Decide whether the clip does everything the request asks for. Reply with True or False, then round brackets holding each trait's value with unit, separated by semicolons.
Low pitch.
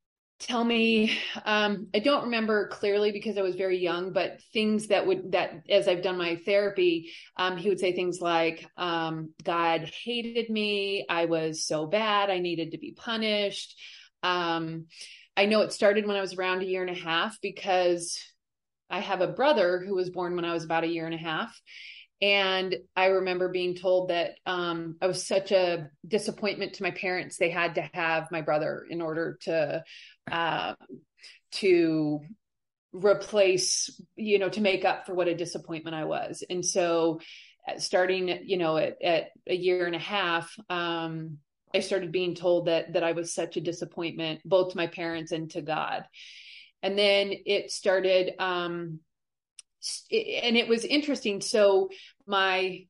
False (185 Hz)